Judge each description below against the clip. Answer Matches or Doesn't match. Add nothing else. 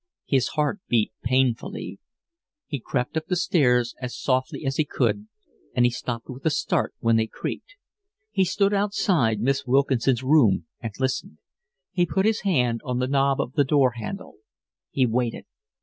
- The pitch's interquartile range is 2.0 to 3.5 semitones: Doesn't match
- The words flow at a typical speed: Matches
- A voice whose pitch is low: Matches